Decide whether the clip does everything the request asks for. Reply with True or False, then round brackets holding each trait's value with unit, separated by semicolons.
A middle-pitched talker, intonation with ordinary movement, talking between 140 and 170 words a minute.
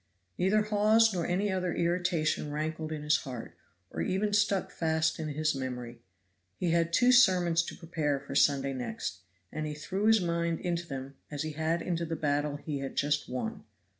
False (160 Hz; 3.8 semitones; 185 wpm)